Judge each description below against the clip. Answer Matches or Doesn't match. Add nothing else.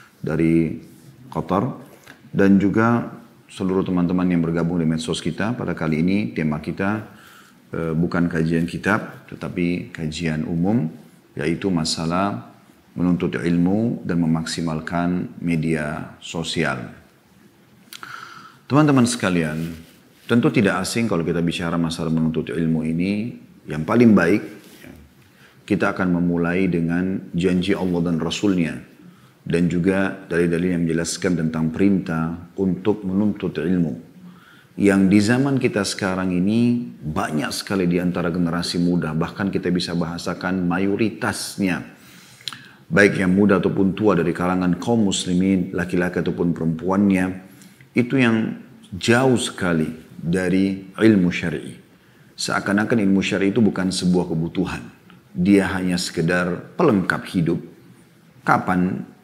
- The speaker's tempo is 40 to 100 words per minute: Doesn't match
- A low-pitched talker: Matches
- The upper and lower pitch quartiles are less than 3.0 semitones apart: Matches